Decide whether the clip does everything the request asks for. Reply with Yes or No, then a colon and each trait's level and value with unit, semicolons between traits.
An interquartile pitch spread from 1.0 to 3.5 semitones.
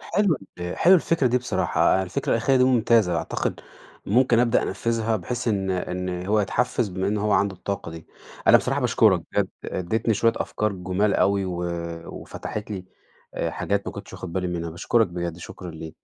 No: average, 4.2 semitones